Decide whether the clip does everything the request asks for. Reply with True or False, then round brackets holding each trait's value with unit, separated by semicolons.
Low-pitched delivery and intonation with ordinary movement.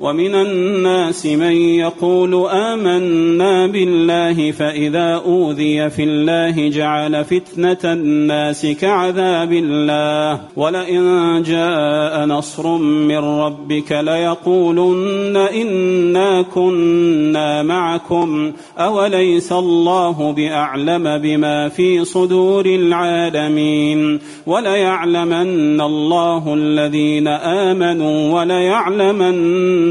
False (170 Hz; 3.1 semitones)